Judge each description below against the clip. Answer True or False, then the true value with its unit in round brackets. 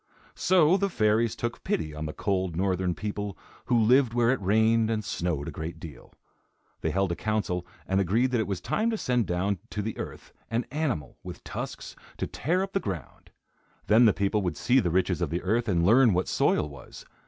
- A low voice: True (105 Hz)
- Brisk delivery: True (210 wpm)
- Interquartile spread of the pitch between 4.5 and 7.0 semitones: True (4.9 semitones)